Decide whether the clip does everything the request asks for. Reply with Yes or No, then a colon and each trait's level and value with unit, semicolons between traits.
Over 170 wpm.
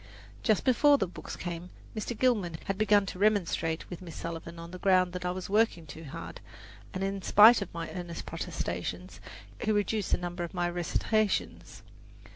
Yes: average, 180 wpm